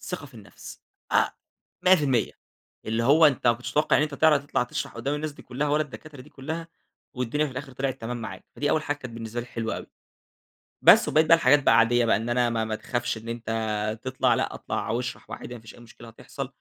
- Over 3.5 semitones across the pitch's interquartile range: Yes, average, 4.2 semitones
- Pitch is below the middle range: Yes, low, 125 Hz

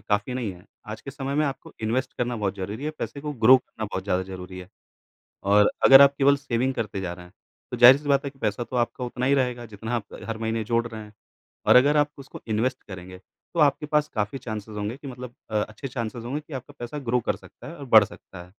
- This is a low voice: Yes, low, 120 Hz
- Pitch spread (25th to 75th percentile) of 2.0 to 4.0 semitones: No, average, 4.4 semitones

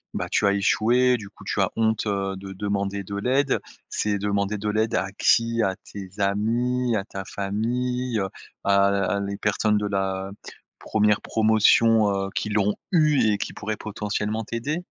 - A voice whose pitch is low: Yes, low, 105 Hz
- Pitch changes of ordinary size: No, narrow, 2.3 semitones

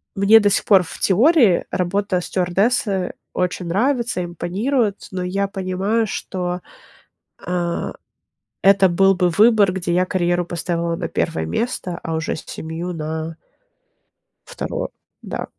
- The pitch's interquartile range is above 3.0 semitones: No, average, 2.7 semitones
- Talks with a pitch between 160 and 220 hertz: Yes, medium, 185 Hz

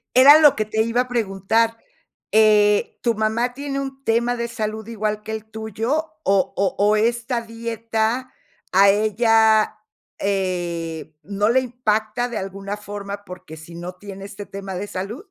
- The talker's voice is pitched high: Yes, high, 215 Hz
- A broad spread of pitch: No, average, 2.8 semitones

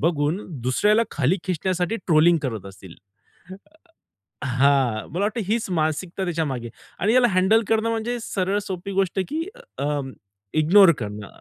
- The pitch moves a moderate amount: No, wide, 6.4 semitones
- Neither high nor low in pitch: Yes, medium, 175 Hz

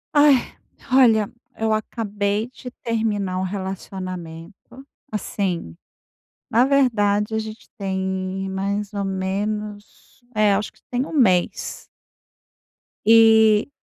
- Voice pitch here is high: Yes, high, 210 Hz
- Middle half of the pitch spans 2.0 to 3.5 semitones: Yes, narrow, 2.6 semitones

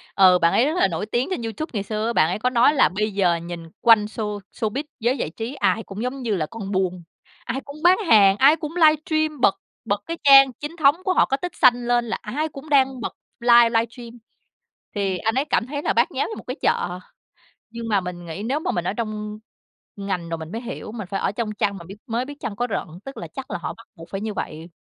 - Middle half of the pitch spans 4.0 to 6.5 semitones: Yes, wide, 5.4 semitones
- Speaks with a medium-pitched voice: No, high, 225 Hz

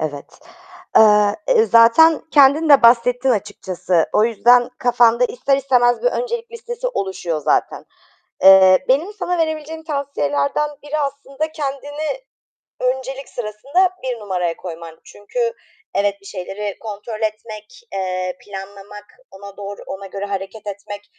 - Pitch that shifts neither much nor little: No, wide, 6.3 semitones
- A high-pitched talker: Yes, high, 230 Hz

